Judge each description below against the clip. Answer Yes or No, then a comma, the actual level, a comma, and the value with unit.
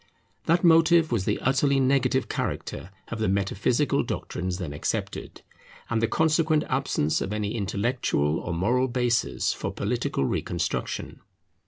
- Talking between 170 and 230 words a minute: No, slow, 135 wpm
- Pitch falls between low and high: No, low, 120 Hz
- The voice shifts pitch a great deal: Yes, wide, 6.0 semitones